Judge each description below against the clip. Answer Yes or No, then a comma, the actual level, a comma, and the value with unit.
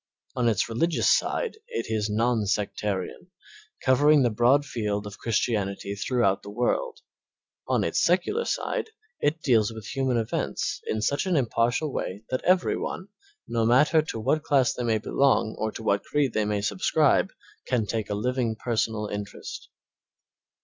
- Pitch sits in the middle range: No, low, 115 Hz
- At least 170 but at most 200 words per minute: No, average, 160 wpm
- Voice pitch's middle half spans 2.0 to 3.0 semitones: No, average, 4.7 semitones